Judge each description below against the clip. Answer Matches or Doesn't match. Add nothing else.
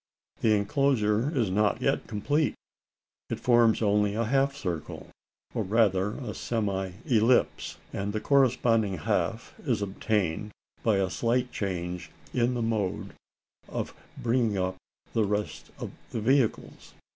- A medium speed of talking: Doesn't match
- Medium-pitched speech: Doesn't match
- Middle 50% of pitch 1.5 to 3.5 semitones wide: Matches